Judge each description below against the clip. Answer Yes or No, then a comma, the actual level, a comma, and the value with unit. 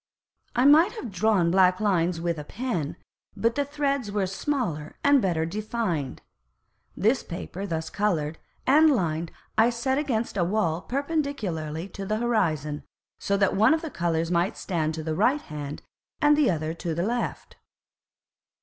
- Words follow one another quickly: No, average, 160 wpm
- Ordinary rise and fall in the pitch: No, wide, 6.9 semitones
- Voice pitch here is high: Yes, high, 195 Hz